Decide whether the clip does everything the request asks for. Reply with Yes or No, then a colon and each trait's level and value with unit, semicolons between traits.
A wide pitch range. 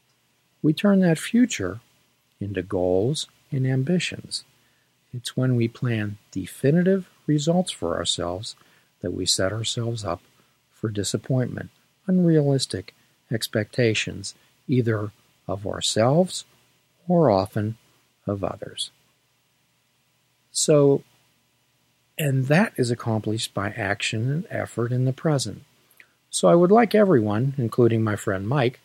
Yes: wide, 5.9 semitones